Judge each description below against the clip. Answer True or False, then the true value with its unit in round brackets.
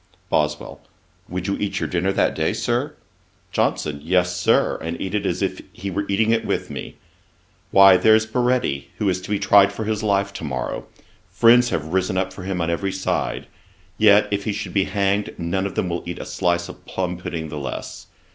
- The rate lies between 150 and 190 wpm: False (205 wpm)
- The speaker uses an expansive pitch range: False (2.7 semitones)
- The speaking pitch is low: True (95 Hz)